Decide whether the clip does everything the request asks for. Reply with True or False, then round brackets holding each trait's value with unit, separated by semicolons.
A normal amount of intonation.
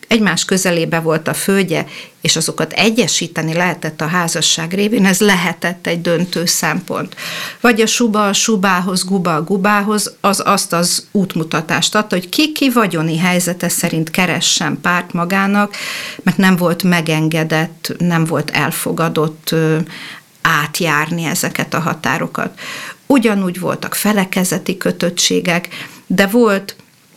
True (3.4 semitones)